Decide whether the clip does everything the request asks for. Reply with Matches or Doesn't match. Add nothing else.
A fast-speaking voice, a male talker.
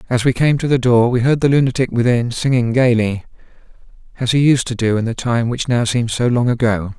Matches